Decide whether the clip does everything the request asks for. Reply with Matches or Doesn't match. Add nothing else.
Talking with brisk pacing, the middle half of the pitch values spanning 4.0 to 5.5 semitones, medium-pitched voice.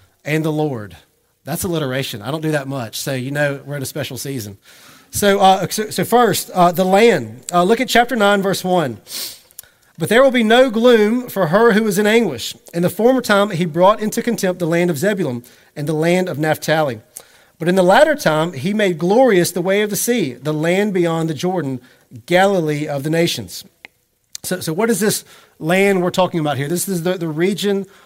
Matches